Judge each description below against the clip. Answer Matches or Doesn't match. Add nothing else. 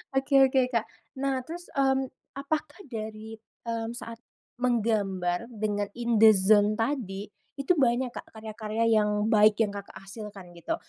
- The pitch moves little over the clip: Doesn't match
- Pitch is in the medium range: Doesn't match